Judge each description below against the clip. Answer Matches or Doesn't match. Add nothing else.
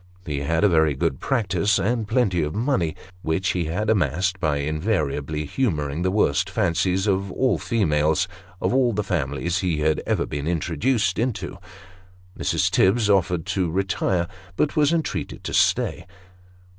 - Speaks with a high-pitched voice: Doesn't match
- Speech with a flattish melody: Doesn't match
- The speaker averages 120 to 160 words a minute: Matches